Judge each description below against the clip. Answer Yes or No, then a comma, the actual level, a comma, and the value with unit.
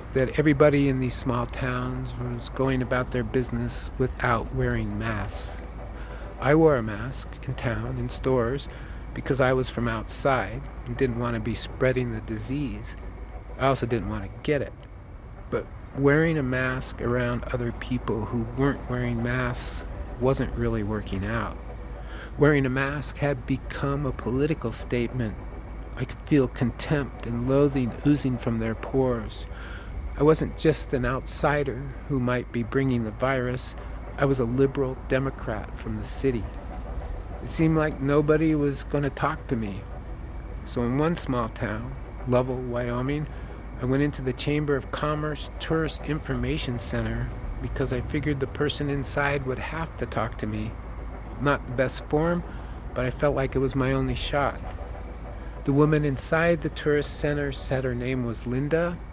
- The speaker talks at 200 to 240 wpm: No, average, 160 wpm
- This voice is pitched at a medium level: No, low, 125 Hz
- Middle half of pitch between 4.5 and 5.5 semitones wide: No, average, 3.5 semitones